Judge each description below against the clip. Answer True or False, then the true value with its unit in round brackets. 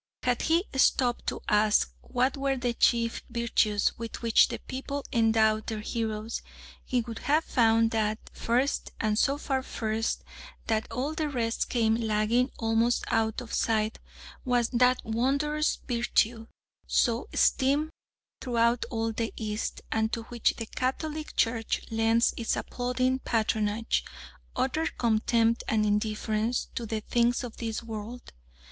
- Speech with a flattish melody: True (2.2 semitones)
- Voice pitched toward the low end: False (230 Hz)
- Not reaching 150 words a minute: True (140 wpm)